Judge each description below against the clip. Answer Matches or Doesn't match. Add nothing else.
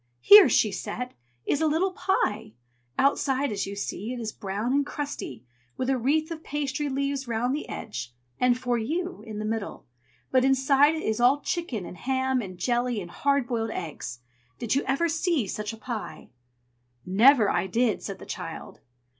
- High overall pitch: Matches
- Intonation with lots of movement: Doesn't match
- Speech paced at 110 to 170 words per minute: Doesn't match